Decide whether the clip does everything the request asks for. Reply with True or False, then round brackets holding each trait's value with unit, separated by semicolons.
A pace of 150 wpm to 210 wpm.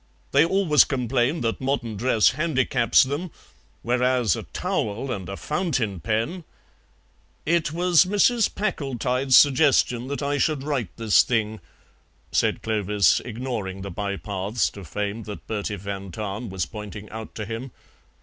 False (140 wpm)